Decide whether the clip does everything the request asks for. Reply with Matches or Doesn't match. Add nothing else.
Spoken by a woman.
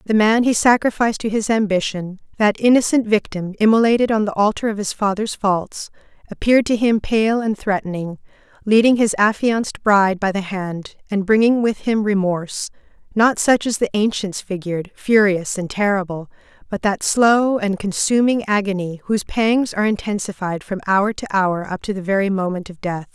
Matches